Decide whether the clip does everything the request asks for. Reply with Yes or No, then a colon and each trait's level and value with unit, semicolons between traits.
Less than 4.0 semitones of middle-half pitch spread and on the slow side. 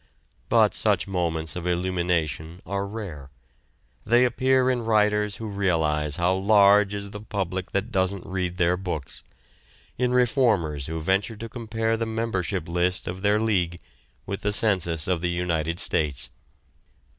No: average, 3.6 semitones; average, 145 wpm